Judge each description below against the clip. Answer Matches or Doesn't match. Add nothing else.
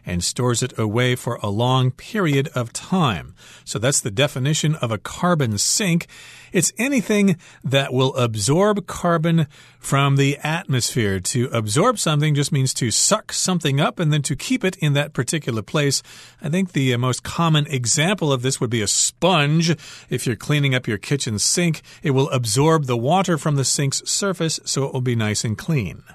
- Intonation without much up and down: Doesn't match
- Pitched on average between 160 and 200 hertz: Doesn't match